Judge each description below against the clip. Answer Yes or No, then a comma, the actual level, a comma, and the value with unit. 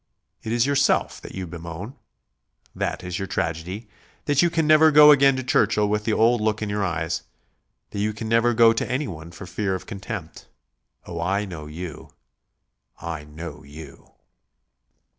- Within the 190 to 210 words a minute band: No, average, 170 wpm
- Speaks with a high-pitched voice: No, low, 100 Hz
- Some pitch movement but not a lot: No, wide, 5.9 semitones